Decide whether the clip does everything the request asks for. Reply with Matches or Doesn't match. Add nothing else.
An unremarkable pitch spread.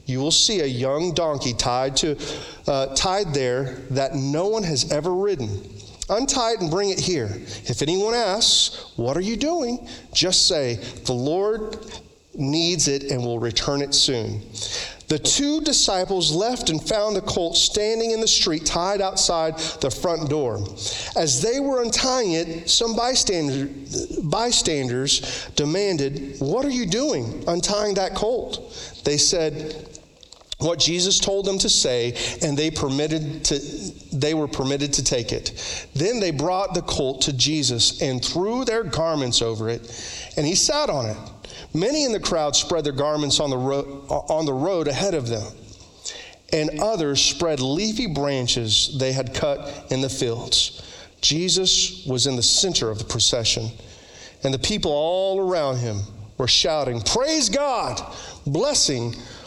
Doesn't match